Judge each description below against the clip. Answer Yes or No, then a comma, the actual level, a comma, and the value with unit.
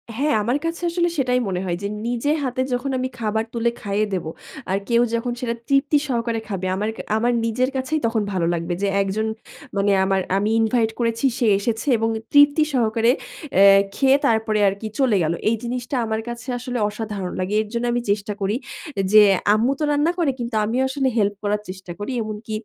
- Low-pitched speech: No, high, 230 Hz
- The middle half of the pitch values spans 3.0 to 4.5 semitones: Yes, average, 3.4 semitones